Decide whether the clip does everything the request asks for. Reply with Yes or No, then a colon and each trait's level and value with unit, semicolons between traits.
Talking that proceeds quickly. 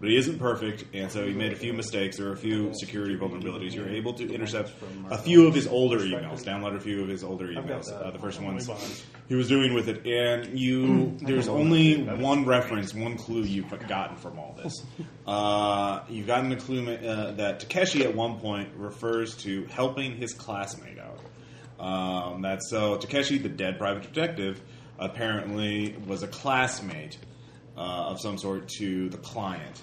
No: average, 190 wpm